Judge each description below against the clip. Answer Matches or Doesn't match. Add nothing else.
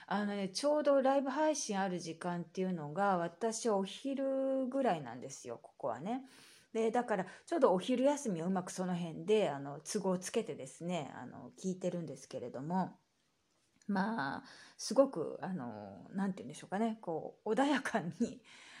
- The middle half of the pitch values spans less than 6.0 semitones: Matches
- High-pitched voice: Matches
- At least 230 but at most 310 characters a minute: Doesn't match